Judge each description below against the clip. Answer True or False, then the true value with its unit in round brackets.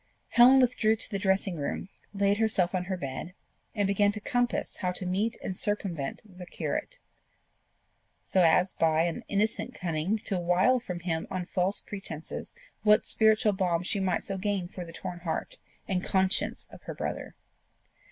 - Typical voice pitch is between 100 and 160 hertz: False (190 Hz)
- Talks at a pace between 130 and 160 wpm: False (170 wpm)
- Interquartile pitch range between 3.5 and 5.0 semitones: False (2.9 semitones)